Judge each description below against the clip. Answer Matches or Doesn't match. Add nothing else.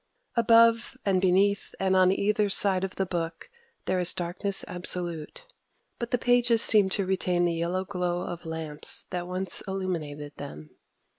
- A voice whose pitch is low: Doesn't match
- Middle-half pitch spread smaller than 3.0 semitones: Matches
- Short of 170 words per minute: Matches